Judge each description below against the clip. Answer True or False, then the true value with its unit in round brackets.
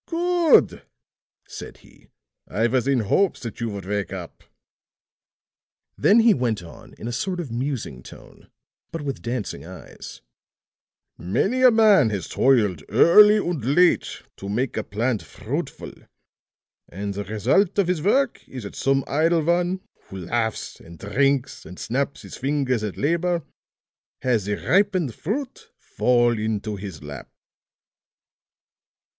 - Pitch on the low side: True (130 Hz)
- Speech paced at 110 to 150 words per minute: True (140 wpm)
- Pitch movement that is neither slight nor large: False (9.0 semitones)